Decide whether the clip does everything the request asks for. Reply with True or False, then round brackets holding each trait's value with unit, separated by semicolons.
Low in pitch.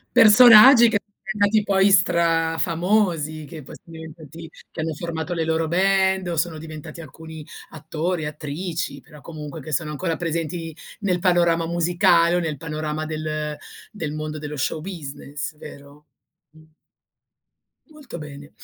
False (165 Hz)